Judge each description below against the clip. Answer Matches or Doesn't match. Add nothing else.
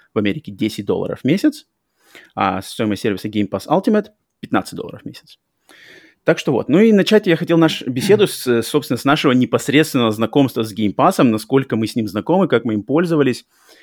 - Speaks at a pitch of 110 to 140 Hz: Matches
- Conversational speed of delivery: Doesn't match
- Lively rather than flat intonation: Matches